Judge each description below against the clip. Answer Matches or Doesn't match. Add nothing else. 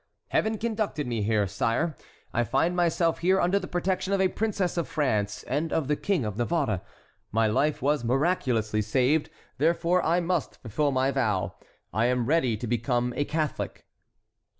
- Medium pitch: Matches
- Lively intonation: Matches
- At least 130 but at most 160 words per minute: Doesn't match